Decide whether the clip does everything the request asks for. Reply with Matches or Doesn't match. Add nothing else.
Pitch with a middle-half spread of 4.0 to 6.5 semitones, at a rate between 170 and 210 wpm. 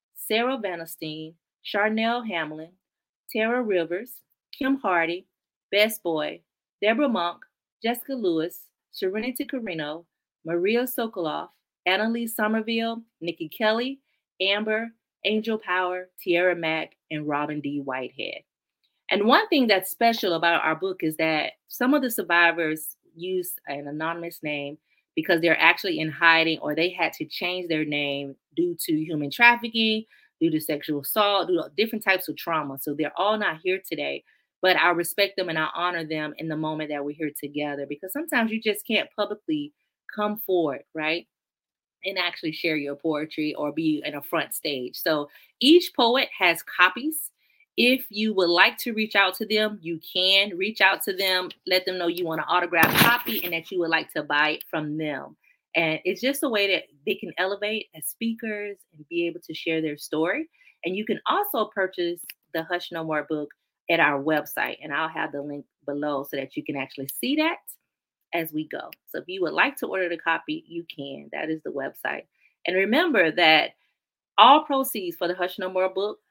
Matches